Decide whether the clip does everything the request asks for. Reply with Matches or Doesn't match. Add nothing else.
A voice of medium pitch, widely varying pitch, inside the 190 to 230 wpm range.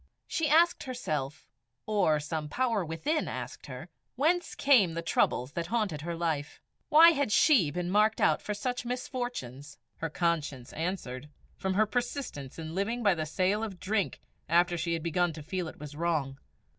Doesn't match